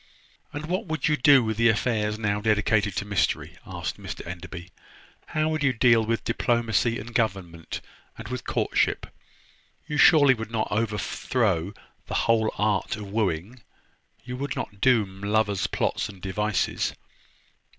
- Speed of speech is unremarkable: Yes, average, 150 wpm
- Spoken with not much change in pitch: No, average, 3.4 semitones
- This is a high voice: No, low, 110 Hz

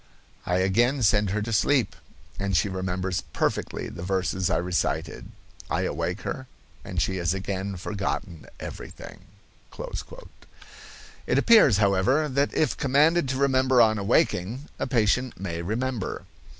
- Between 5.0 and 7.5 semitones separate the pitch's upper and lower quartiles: Yes, wide, 5.6 semitones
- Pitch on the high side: No, low, 105 Hz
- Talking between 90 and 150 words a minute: Yes, slow, 135 wpm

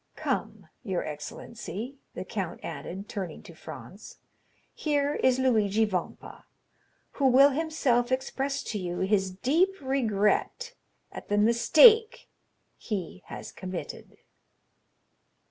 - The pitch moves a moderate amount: No, wide, 6.1 semitones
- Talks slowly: Yes, slow, 110 wpm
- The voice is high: Yes, high, 235 Hz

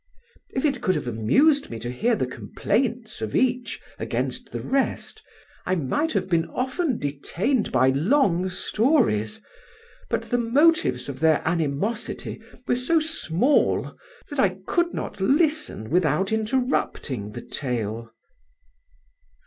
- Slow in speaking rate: Yes, slow, 130 wpm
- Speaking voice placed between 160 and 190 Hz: No, high, 205 Hz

